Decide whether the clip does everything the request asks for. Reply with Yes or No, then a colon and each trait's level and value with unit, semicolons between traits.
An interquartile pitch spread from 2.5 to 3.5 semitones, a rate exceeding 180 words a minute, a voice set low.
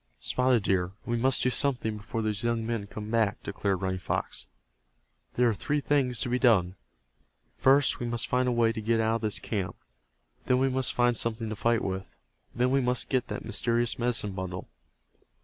Yes: average, 2.9 semitones; average, 195 wpm; low, 115 Hz